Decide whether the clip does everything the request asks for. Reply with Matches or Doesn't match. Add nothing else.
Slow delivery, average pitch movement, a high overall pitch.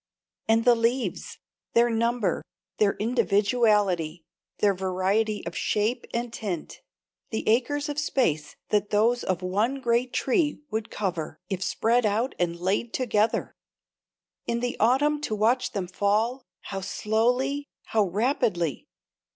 Matches